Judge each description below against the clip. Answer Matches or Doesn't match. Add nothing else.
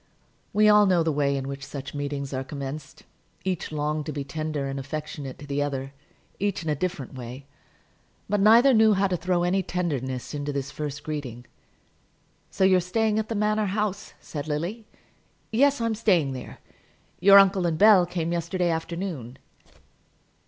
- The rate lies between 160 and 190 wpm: Matches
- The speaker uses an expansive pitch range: Matches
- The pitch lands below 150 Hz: Doesn't match